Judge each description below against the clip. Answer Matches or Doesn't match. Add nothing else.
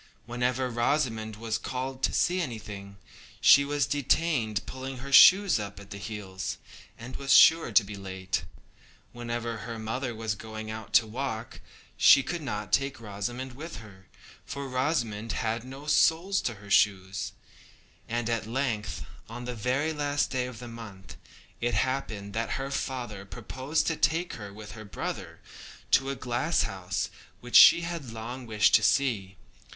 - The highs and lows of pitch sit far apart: Doesn't match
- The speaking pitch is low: Matches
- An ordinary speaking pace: Matches